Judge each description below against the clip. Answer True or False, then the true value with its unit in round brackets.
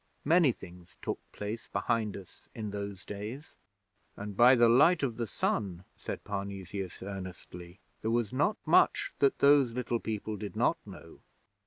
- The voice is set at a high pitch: False (105 Hz)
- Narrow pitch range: False (3.8 semitones)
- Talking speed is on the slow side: False (155 wpm)